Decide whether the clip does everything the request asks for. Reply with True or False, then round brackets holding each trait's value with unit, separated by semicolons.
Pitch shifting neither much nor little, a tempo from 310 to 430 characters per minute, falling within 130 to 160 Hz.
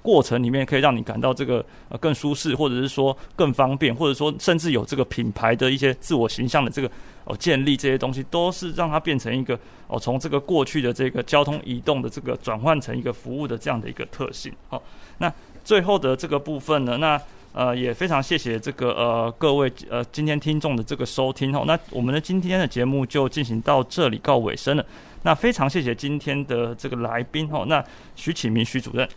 True (3.6 semitones; 330 characters per minute; 135 Hz)